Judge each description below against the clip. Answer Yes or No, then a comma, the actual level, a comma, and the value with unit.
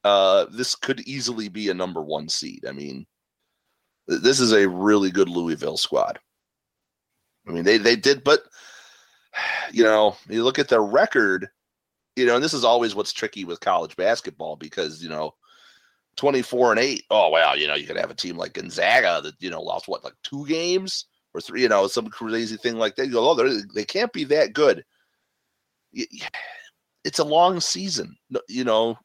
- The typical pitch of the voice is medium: No, low, 115 Hz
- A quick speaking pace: No, average, 190 wpm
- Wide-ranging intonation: Yes, wide, 6.4 semitones